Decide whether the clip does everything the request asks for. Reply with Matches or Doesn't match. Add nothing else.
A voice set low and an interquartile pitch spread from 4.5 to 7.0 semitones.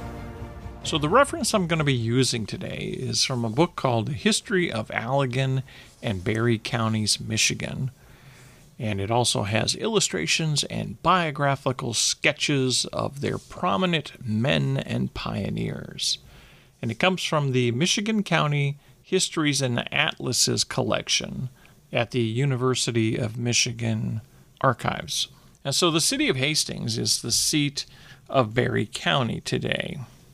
Matches